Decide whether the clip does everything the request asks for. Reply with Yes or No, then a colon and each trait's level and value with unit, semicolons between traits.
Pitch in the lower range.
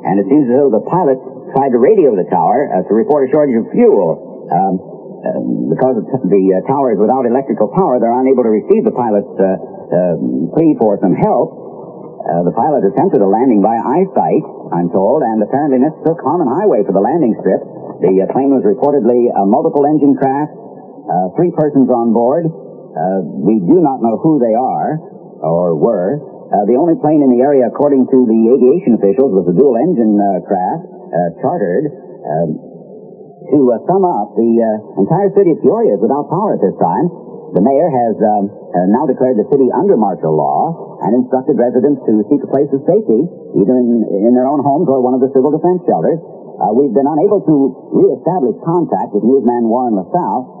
Yes: low, 125 Hz